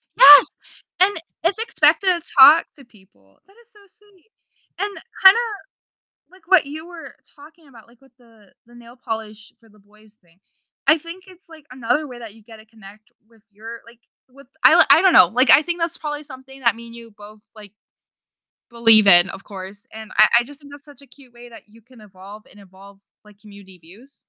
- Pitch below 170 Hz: No, high, 235 Hz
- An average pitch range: No, wide, 6.0 semitones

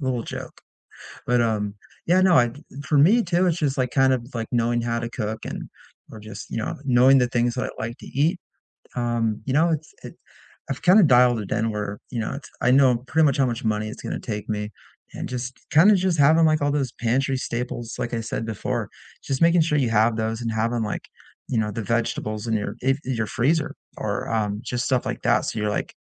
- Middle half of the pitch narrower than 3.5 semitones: No, average, 3.8 semitones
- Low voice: Yes, low, 120 Hz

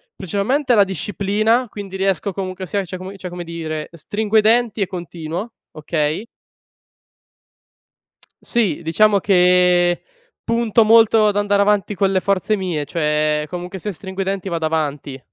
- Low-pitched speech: No, high, 190 Hz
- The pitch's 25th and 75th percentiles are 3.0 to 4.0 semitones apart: Yes, average, 3.5 semitones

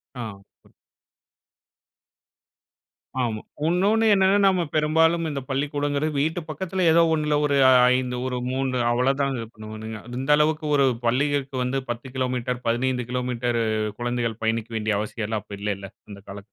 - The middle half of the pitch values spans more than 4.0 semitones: Yes, average, 4.5 semitones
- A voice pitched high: No, low, 130 Hz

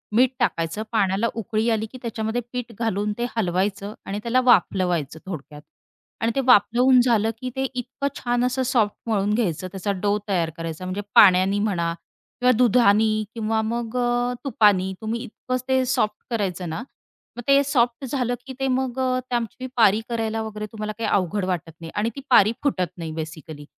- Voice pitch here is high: Yes, high, 220 Hz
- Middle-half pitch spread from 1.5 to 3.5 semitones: No, average, 4.2 semitones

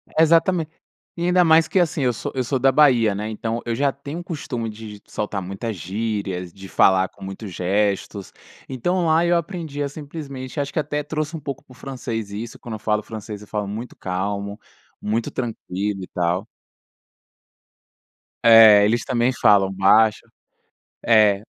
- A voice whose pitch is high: No, low, 115 Hz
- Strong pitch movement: Yes, wide, 5.8 semitones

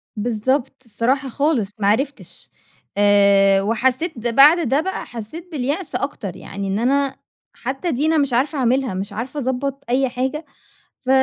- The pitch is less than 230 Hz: No, very high, 260 Hz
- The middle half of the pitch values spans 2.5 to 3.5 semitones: No, average, 4.3 semitones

